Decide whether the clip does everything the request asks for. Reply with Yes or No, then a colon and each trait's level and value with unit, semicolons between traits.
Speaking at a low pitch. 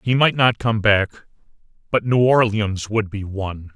Yes: low, 110 Hz